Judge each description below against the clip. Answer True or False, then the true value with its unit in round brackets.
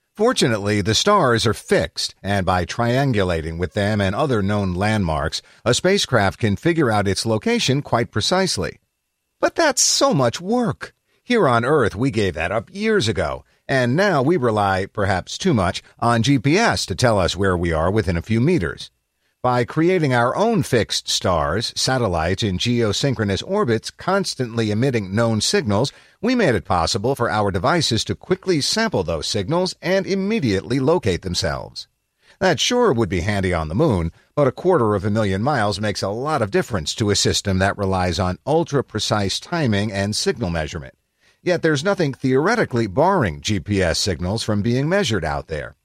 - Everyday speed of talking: True (170 wpm)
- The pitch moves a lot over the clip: True (6.4 semitones)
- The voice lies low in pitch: True (110 Hz)